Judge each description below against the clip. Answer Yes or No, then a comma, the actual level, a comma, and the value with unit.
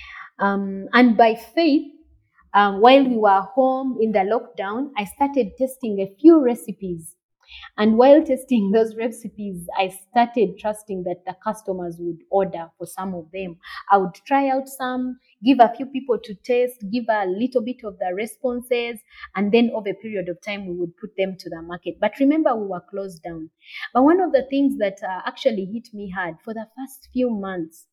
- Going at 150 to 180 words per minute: No, average, 190 wpm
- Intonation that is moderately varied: Yes, average, 4.7 semitones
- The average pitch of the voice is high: Yes, high, 215 Hz